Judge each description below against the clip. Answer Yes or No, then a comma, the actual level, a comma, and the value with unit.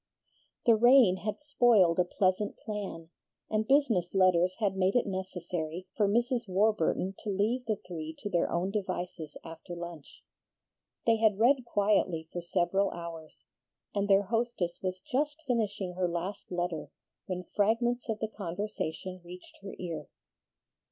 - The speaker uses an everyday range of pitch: Yes, average, 3.8 semitones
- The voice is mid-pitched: No, high, 195 Hz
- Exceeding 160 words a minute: No, average, 145 wpm